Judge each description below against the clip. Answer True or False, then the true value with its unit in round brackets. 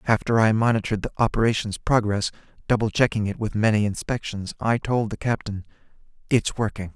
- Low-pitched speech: True (110 Hz)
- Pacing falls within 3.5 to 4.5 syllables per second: False (5.8 syllables/s)